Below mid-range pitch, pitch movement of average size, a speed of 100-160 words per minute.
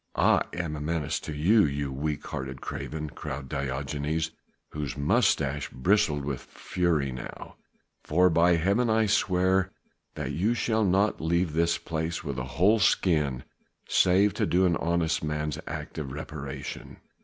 Yes: very low, 80 Hz; average, 3.9 semitones; average, 150 wpm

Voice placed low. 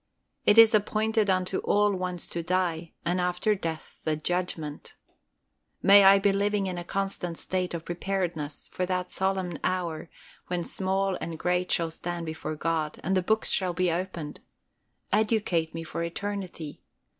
No: medium, 180 Hz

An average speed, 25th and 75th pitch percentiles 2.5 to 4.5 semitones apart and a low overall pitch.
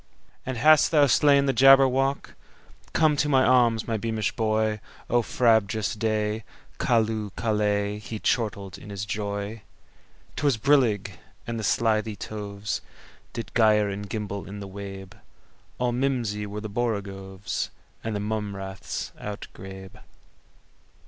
No: slow, 115 wpm; average, 2.8 semitones; low, 110 Hz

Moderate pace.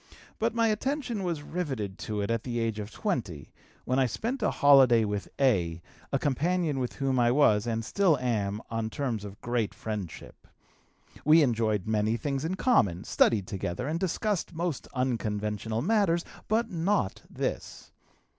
Yes: average, 160 wpm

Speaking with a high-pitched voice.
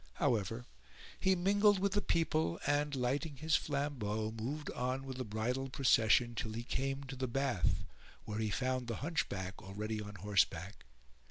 No: low, 125 Hz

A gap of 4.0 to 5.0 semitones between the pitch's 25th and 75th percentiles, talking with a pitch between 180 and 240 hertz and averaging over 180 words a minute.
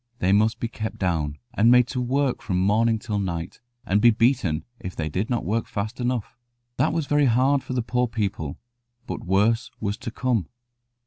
No: average, 4.4 semitones; low, 110 Hz; average, 195 wpm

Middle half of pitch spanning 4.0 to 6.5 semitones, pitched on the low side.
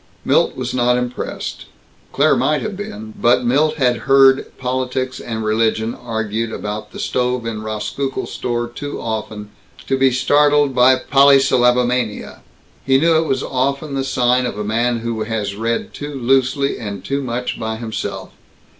No: average, 3.1 semitones; low, 125 Hz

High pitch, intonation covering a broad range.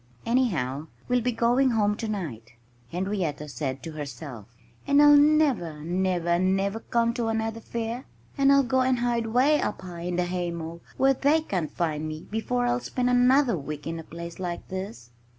Yes: high, 200 Hz; wide, 7.0 semitones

